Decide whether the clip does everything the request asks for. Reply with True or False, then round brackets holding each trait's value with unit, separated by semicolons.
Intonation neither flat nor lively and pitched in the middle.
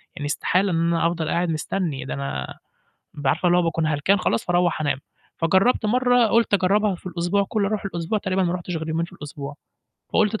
True (3.8 semitones; 175 Hz)